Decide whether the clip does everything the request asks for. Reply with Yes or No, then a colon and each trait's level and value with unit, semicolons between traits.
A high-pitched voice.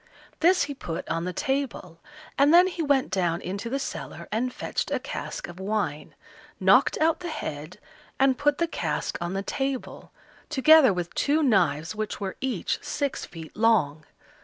Yes: high, 230 Hz